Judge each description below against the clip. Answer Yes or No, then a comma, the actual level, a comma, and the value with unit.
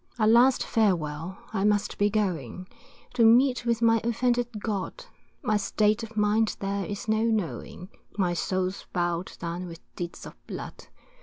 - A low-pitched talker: No, high, 210 Hz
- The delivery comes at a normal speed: Yes, average, 155 wpm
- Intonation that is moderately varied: Yes, average, 3.6 semitones